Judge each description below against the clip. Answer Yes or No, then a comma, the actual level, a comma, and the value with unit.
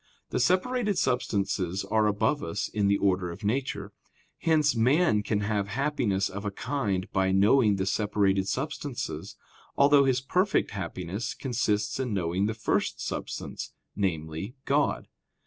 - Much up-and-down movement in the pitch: Yes, wide, 5.7 semitones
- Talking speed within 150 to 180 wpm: No, average, 140 wpm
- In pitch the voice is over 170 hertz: No, low, 105 Hz